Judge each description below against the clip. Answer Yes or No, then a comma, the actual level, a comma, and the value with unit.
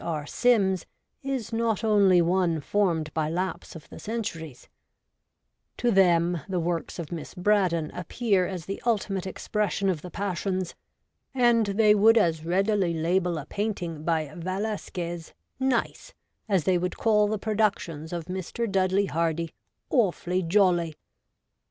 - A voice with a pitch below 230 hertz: Yes, medium, 185 Hz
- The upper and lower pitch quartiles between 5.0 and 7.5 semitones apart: No, average, 3.8 semitones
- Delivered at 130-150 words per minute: Yes, average, 145 wpm